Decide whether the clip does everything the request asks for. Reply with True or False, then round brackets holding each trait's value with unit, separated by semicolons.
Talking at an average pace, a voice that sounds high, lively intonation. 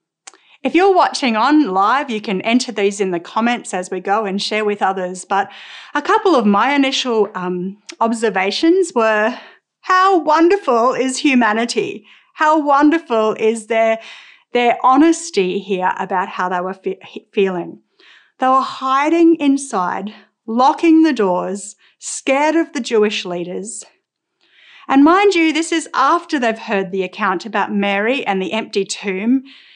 True (145 wpm; 230 Hz; 6.9 semitones)